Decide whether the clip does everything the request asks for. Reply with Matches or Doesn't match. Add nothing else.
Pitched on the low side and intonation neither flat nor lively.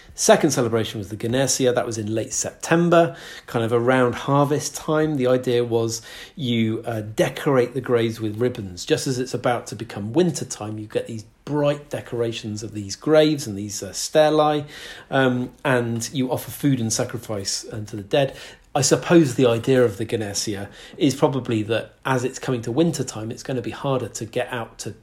Matches